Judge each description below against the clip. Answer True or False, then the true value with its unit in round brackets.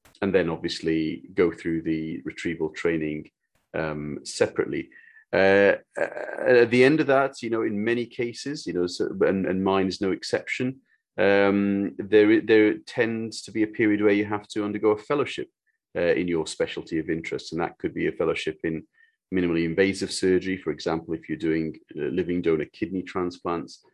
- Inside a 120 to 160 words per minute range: False (180 wpm)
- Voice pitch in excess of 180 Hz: False (105 Hz)